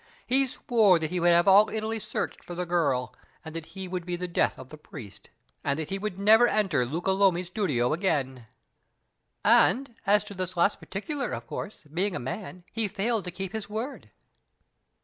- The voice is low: No, medium, 185 Hz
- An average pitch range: Yes, average, 4.1 semitones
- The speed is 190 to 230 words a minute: Yes, average, 195 wpm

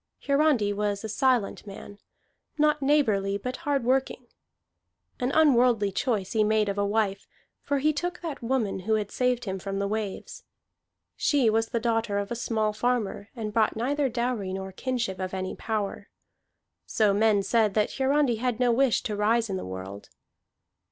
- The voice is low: No, high, 225 Hz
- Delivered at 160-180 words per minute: Yes, average, 170 wpm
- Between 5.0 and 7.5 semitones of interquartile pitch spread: No, average, 4.0 semitones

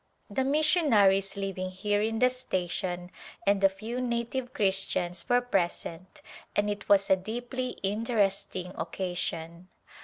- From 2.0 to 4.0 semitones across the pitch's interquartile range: No, average, 4.4 semitones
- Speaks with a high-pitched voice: Yes, high, 200 Hz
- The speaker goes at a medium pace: No, slow, 125 wpm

